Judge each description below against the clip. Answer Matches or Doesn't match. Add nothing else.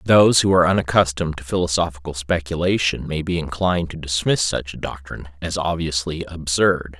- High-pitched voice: Doesn't match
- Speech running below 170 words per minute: Matches